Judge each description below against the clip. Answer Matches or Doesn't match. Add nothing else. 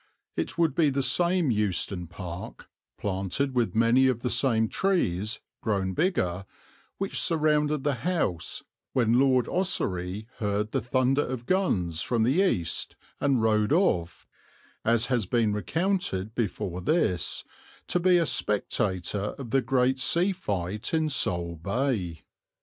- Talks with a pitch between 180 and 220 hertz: Doesn't match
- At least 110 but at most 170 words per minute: Matches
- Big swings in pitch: Matches